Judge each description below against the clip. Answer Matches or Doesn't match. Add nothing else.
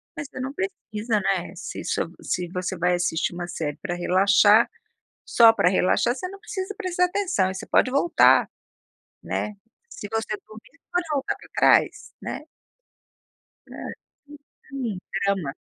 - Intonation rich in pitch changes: Matches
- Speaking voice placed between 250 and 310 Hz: Doesn't match